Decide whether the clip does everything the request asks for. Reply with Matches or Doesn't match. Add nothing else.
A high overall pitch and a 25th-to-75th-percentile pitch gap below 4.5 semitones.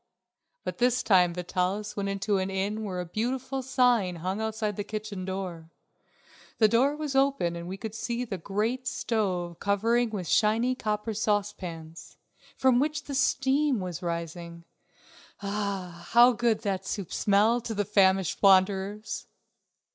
Matches